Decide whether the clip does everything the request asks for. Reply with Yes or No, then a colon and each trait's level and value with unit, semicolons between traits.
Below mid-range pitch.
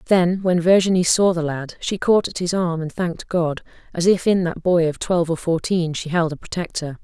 No: medium, 170 Hz